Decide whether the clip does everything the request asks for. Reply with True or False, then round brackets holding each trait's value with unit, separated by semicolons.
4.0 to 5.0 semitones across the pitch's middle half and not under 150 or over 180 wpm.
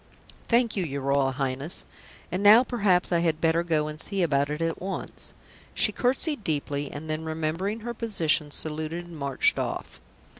True (4.7 semitones; 175 wpm)